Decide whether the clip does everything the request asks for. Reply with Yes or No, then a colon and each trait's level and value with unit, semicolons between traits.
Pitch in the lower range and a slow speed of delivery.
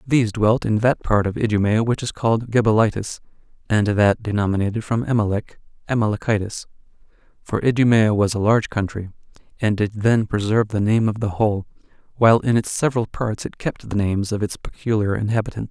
No: low, 110 Hz; average, 170 wpm